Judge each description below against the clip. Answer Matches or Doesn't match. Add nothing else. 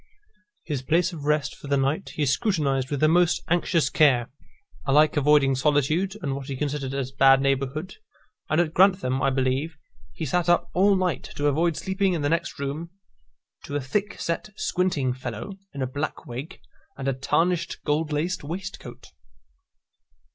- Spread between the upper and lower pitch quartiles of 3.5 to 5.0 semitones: Matches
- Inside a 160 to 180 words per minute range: Matches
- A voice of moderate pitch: Matches